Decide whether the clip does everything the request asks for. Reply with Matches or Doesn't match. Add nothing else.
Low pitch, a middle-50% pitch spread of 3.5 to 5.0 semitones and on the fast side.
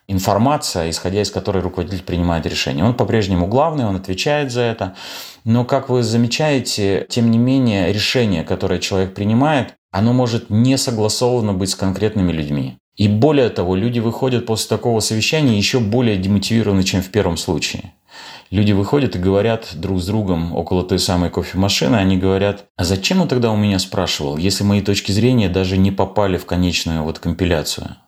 Matches